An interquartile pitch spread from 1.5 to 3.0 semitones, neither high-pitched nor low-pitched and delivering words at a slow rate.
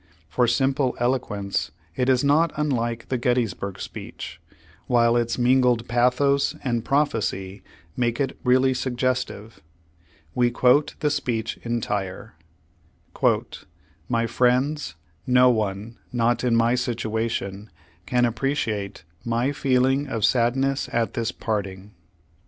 No: narrow, 2.4 semitones; low, 120 Hz; slow, 115 wpm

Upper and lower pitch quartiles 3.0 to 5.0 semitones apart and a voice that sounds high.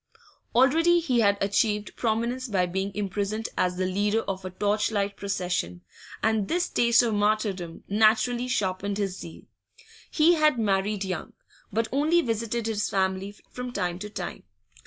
Yes: average, 3.5 semitones; high, 210 Hz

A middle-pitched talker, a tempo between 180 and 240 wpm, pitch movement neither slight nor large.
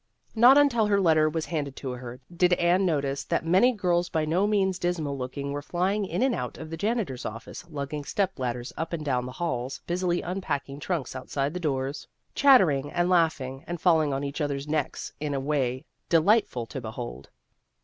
Yes: medium, 155 Hz; average, 190 wpm; average, 4.7 semitones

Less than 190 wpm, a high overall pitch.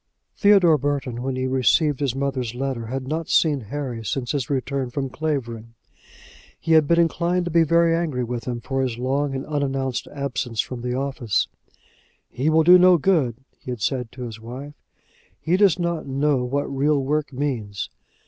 No: average, 180 wpm; low, 135 Hz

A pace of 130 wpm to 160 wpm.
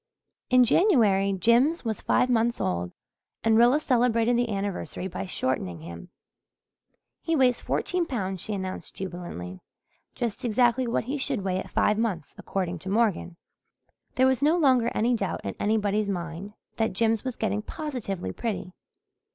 Yes: average, 150 wpm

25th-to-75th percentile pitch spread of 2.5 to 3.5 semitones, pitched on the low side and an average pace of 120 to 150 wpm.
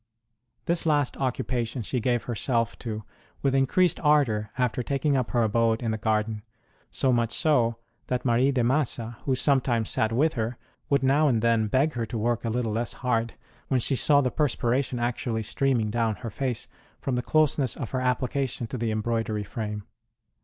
No: average, 2.9 semitones; low, 120 Hz; average, 185 wpm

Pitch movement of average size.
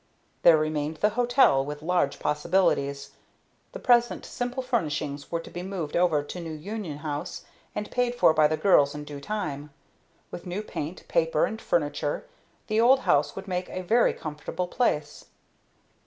No: wide, 6.1 semitones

